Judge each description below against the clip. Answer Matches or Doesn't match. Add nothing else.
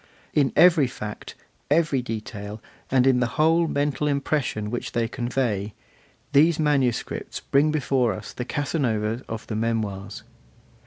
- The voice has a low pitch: Matches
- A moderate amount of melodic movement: Matches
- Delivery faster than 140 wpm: Doesn't match